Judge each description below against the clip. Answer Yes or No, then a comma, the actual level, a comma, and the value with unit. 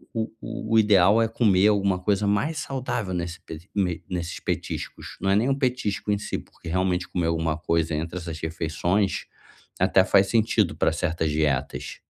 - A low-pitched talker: Yes, very low, 95 Hz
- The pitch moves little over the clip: No, average, 3.8 semitones